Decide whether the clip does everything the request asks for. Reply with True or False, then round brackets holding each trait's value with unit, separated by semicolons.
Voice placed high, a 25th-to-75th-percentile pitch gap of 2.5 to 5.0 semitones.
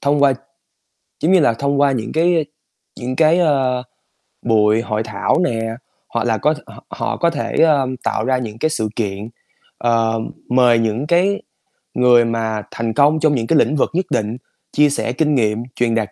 False (125 Hz; 4.7 semitones)